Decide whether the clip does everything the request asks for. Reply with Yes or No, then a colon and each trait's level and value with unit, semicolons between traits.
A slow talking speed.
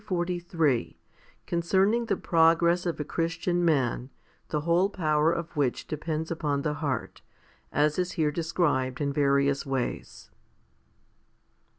Yes: slow, 125 wpm